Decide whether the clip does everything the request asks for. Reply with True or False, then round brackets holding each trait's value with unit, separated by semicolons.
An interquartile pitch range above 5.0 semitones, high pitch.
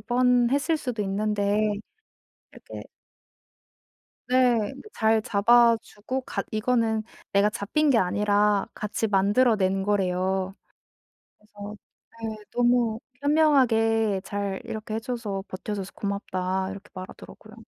False (3.2 semitones; 215 Hz)